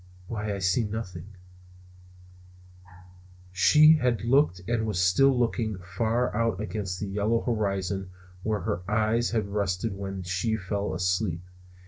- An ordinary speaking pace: No, slow, 130 wpm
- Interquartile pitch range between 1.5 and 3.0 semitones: No, average, 3.6 semitones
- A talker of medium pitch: No, low, 105 Hz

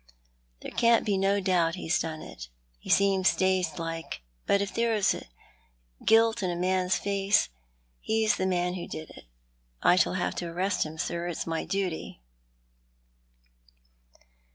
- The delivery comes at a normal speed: Yes, average, 155 wpm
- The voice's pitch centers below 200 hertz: Yes, medium, 185 Hz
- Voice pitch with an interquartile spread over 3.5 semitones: No, narrow, 2.6 semitones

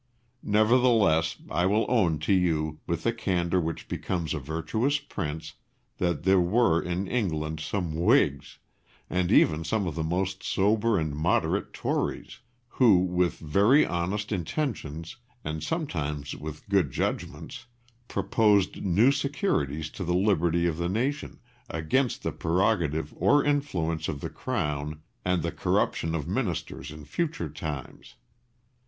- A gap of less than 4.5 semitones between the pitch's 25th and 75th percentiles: No, average, 5.2 semitones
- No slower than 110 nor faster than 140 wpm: Yes, slow, 135 wpm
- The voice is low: Yes, very low, 90 Hz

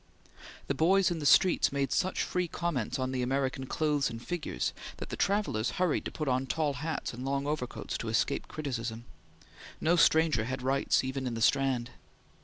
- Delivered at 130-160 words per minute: No, average, 185 wpm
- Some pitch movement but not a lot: Yes, average, 3.9 semitones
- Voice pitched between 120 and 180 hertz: Yes, medium, 140 Hz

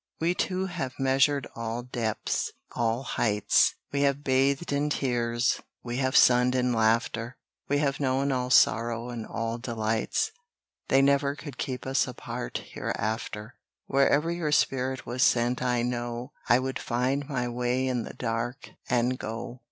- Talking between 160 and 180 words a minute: No, average, 150 wpm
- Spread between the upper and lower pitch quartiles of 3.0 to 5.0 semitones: No, narrow, 2.6 semitones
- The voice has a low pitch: Yes, low, 125 Hz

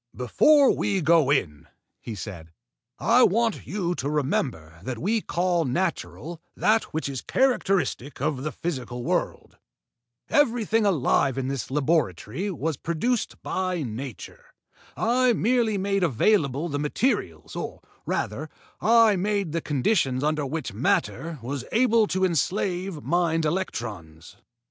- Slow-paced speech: Yes, slow, 130 wpm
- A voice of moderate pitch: Yes, medium, 160 Hz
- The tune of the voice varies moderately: No, wide, 7.4 semitones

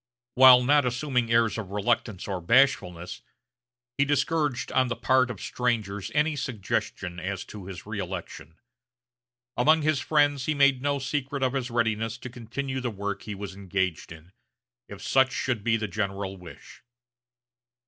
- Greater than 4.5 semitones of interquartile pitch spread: Yes, average, 5.1 semitones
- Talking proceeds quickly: No, average, 155 wpm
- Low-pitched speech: Yes, low, 120 Hz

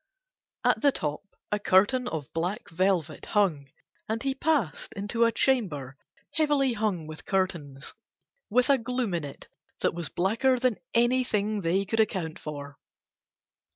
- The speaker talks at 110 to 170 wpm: Yes, average, 145 wpm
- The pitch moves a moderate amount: No, wide, 6.9 semitones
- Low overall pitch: No, high, 200 Hz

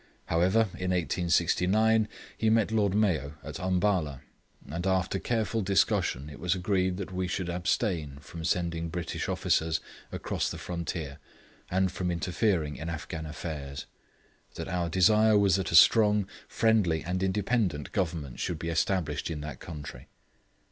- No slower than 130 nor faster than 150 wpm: Yes, average, 145 wpm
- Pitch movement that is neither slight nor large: Yes, average, 3.4 semitones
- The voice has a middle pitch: No, very low, 90 Hz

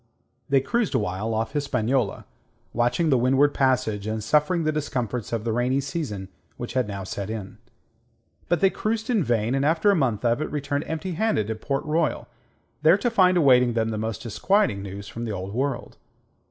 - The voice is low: Yes, low, 130 Hz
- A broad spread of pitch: Yes, wide, 5.7 semitones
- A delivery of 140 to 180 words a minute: No, average, 190 wpm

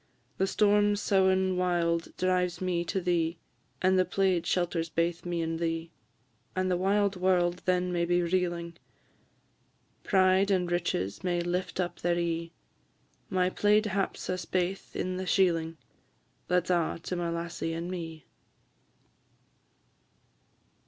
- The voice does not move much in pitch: Yes, narrow, 1.6 semitones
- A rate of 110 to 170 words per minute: Yes, slow, 135 wpm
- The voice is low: No, medium, 180 Hz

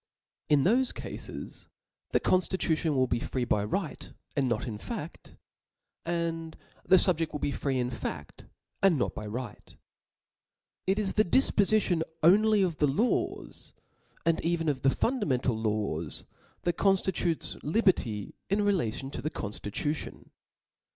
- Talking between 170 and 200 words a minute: No, slow, 135 wpm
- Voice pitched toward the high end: No, medium, 160 Hz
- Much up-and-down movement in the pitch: Yes, wide, 7.1 semitones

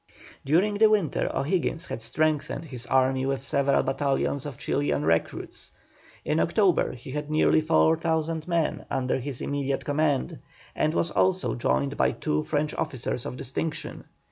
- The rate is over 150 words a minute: No, average, 145 wpm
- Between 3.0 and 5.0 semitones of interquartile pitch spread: Yes, average, 3.4 semitones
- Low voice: No, medium, 145 Hz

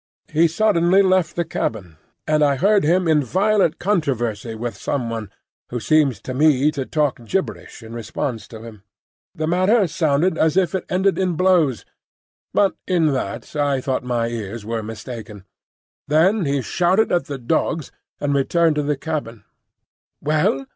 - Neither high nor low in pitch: Yes, medium, 150 Hz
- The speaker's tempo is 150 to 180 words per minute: Yes, average, 160 wpm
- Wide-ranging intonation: Yes, wide, 6.3 semitones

